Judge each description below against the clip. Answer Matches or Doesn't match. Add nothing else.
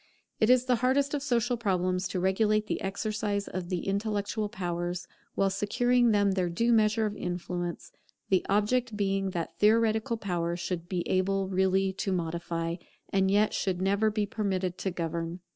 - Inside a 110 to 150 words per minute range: Doesn't match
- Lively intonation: Doesn't match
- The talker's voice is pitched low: Doesn't match